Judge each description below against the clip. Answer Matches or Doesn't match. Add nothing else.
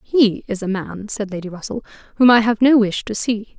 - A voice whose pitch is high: Matches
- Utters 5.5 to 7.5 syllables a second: Doesn't match